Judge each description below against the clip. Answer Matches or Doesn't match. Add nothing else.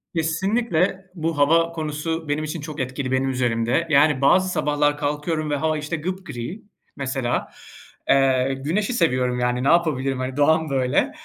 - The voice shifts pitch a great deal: Doesn't match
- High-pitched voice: Doesn't match